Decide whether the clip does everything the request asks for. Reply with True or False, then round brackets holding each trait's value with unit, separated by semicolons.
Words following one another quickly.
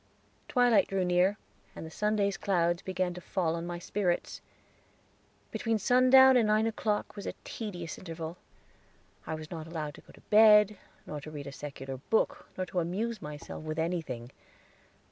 False (165 wpm)